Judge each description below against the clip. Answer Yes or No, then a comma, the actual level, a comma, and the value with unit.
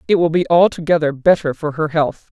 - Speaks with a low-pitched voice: No, medium, 160 Hz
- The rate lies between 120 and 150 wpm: No, average, 200 wpm